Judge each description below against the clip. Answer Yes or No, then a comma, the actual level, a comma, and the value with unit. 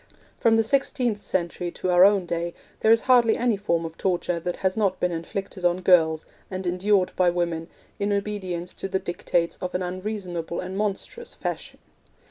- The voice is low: No, medium, 185 Hz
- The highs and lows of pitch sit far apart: No, average, 2.8 semitones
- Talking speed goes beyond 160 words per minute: Yes, average, 180 wpm